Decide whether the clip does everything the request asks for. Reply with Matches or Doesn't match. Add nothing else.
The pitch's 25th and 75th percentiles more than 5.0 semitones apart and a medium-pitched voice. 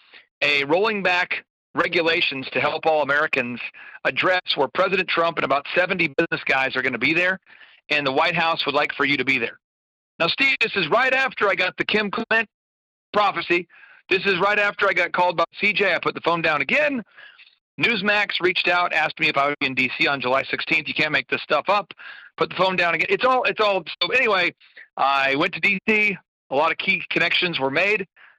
Matches